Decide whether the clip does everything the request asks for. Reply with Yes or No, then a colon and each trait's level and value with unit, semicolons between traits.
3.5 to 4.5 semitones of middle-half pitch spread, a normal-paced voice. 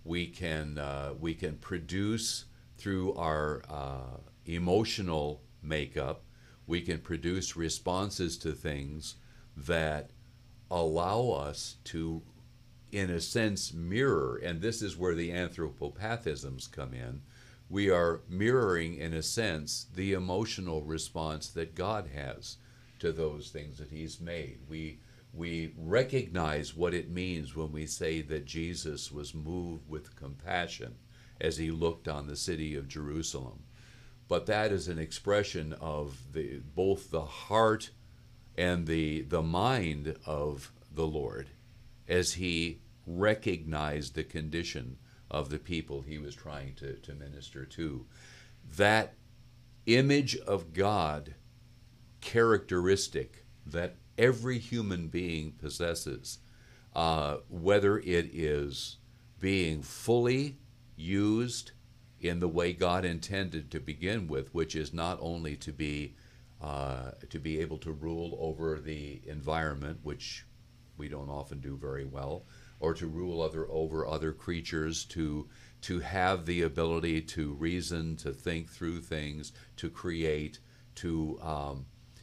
No: average, 4.2 semitones; slow, 130 wpm